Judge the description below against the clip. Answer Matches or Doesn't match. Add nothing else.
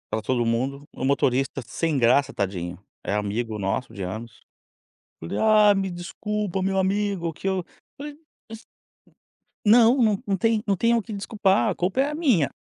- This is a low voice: Doesn't match